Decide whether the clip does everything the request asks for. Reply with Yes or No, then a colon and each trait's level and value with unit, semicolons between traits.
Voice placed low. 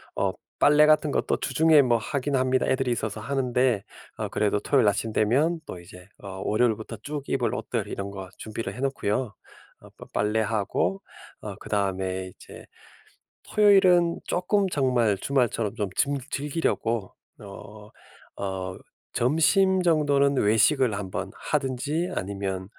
Yes: low, 120 Hz